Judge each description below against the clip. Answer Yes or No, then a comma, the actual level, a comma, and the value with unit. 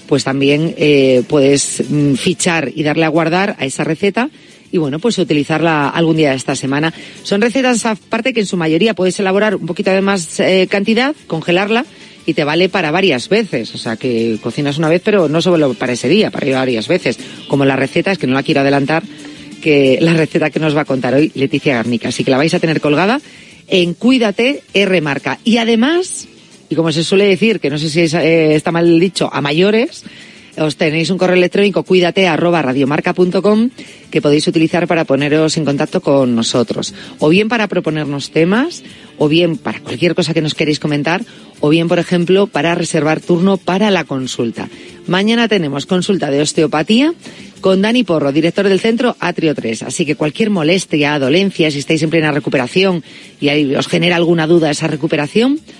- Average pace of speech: No, fast, 195 wpm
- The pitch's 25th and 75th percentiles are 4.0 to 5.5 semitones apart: Yes, average, 4.5 semitones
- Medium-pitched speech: Yes, medium, 165 Hz